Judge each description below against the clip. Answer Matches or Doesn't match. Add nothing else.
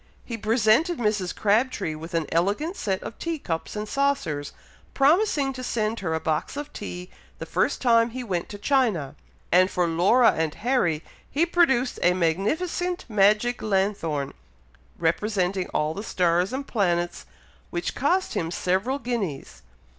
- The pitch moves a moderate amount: Doesn't match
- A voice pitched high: Matches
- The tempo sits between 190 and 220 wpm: Doesn't match